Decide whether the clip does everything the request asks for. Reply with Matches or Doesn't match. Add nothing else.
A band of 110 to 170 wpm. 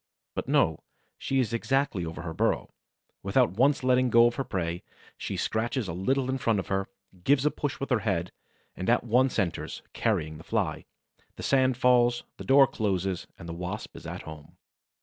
Doesn't match